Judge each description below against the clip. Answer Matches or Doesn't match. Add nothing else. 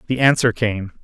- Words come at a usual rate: Matches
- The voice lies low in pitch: Matches